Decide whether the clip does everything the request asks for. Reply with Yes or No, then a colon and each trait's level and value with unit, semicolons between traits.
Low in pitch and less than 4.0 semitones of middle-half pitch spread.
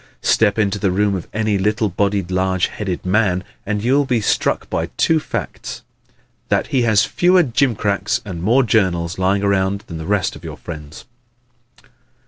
Yes: low, 100 Hz; average, 3.0 semitones